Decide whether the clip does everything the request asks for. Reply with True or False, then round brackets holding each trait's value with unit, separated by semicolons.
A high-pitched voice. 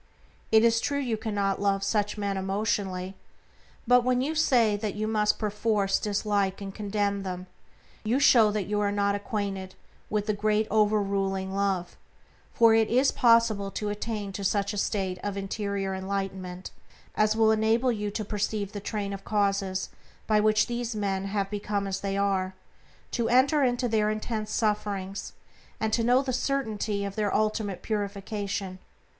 True (205 Hz)